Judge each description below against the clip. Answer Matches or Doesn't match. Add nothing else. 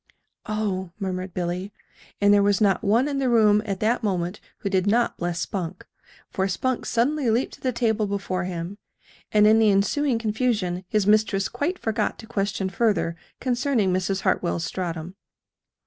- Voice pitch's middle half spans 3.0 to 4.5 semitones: Matches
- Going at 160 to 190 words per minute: Matches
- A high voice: Matches